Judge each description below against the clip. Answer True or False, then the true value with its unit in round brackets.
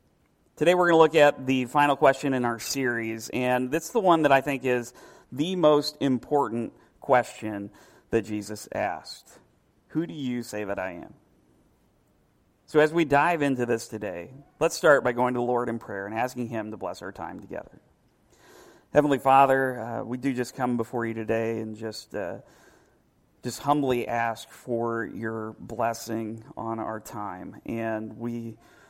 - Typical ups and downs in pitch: True (3.6 semitones)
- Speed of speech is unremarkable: True (170 wpm)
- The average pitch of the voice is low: True (125 Hz)